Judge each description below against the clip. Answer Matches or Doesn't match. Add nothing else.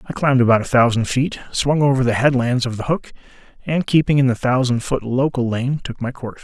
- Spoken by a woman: Doesn't match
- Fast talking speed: Matches